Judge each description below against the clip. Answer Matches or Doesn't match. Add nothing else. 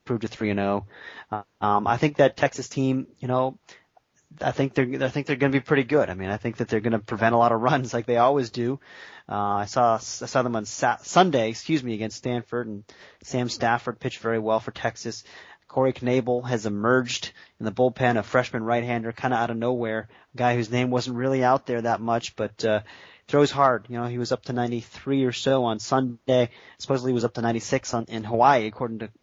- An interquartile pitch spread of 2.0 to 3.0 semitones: Matches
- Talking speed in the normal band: Doesn't match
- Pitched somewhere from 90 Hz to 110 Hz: Doesn't match